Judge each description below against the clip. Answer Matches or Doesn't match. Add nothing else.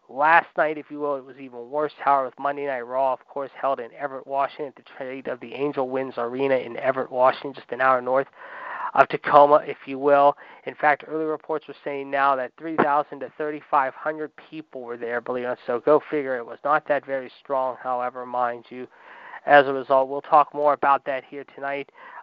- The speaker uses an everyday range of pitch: Doesn't match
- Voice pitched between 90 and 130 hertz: Doesn't match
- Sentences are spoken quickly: Matches